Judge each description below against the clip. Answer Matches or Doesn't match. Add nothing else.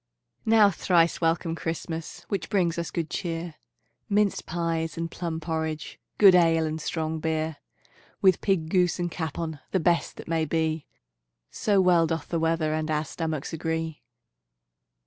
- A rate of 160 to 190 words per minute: Doesn't match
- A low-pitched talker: Doesn't match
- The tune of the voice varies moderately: Doesn't match